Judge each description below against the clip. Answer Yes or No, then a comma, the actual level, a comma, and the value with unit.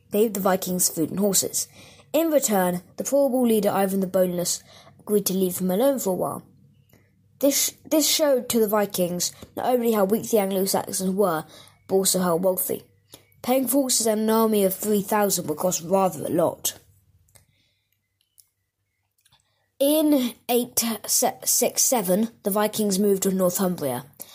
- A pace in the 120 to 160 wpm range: Yes, average, 150 wpm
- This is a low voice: No, high, 195 Hz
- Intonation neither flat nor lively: Yes, average, 4.1 semitones